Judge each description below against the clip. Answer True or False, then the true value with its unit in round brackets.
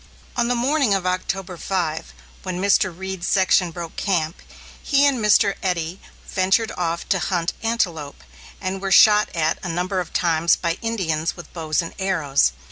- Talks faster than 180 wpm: False (165 wpm)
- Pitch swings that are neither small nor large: True (3.0 semitones)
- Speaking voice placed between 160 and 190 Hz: True (185 Hz)